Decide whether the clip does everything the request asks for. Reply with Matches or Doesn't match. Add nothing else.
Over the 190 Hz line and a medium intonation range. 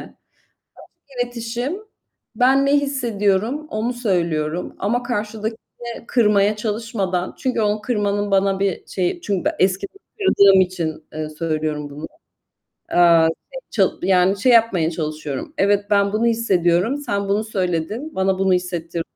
Matches